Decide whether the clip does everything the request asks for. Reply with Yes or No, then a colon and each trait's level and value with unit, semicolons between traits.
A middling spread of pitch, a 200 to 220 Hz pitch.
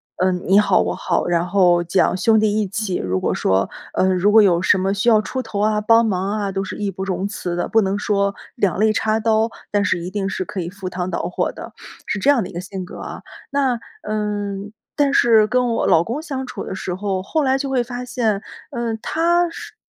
Yes: average, 3.4 semitones; high, 205 Hz